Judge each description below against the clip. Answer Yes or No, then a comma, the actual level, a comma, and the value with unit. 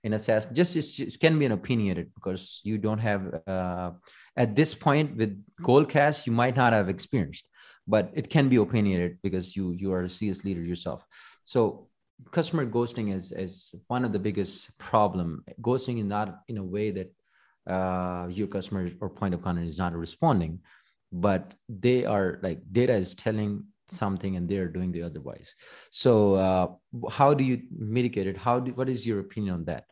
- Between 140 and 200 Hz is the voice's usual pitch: No, low, 105 Hz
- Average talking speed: Yes, average, 185 wpm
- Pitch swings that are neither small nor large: Yes, average, 4.7 semitones